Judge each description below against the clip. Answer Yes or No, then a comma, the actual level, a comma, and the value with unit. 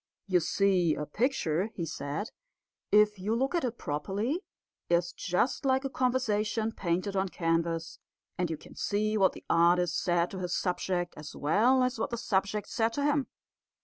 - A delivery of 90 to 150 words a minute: No, average, 175 wpm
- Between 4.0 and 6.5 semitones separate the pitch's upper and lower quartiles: Yes, average, 4.9 semitones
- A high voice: Yes, high, 195 Hz